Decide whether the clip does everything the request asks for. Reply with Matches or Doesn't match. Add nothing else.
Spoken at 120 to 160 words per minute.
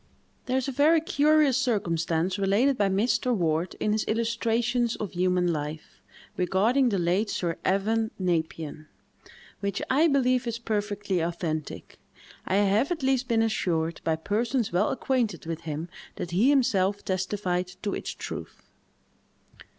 Matches